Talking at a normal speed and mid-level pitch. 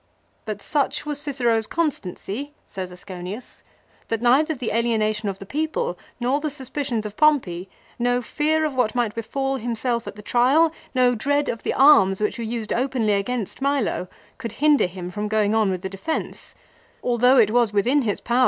No: average, 185 wpm; high, 240 Hz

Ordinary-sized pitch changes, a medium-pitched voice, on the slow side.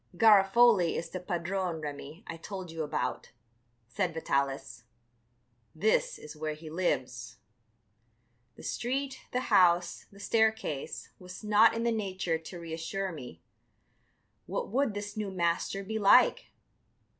Yes: average, 4.7 semitones; medium, 180 Hz; slow, 130 wpm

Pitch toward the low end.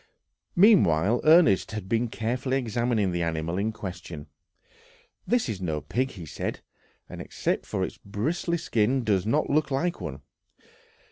Yes: low, 110 Hz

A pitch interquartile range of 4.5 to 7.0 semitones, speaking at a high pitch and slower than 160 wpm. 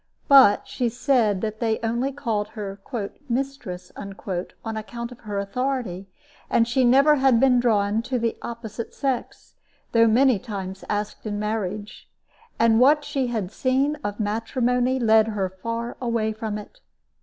No: average, 3.3 semitones; high, 230 Hz; average, 150 wpm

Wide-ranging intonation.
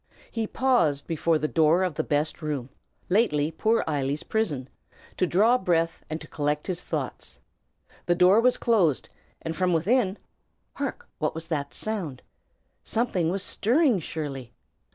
Yes: wide, 6.1 semitones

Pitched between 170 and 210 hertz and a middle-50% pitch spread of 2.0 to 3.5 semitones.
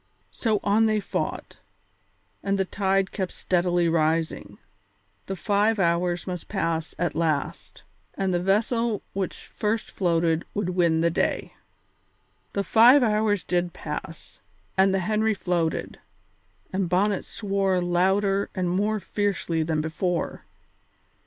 Yes: high, 190 Hz; average, 3.0 semitones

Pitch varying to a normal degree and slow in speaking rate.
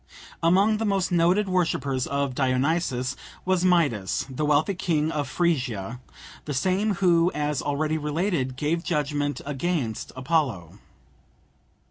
Yes: average, 4.7 semitones; slow, 120 wpm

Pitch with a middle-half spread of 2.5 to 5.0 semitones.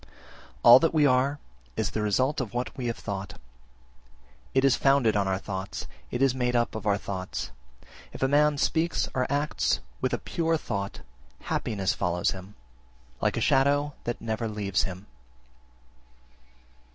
No: wide, 5.6 semitones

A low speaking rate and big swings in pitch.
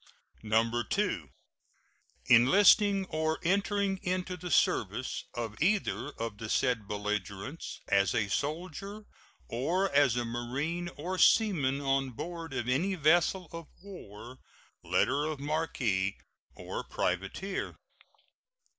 Yes: slow, 110 wpm; wide, 7.4 semitones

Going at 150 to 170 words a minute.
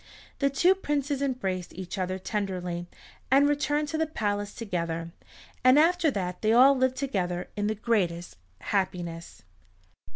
No: average, 140 wpm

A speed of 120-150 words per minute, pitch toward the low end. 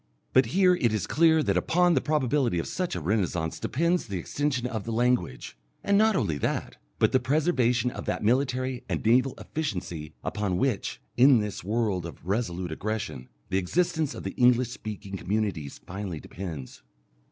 No: average, 170 wpm; low, 115 Hz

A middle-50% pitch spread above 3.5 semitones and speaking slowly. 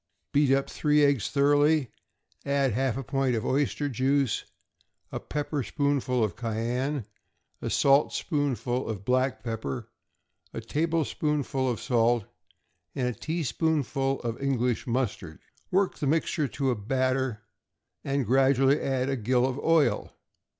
No: average, 2.9 semitones; slow, 130 wpm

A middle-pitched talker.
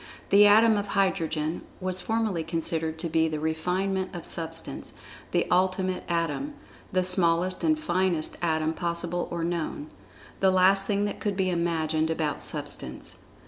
Yes: medium, 175 Hz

